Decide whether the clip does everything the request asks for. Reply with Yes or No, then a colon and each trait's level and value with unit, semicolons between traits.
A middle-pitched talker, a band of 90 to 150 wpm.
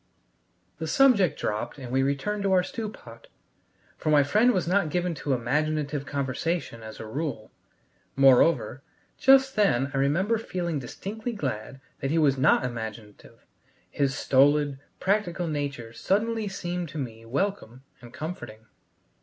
Yes: medium, 145 Hz; average, 145 wpm